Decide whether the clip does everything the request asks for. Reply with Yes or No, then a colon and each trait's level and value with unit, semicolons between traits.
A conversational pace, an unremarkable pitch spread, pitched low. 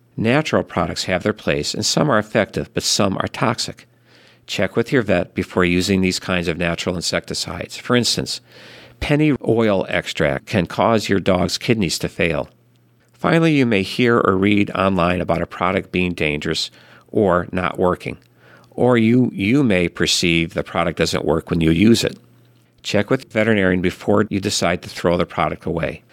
Yes: average, 175 wpm; average, 4.2 semitones; very low, 95 Hz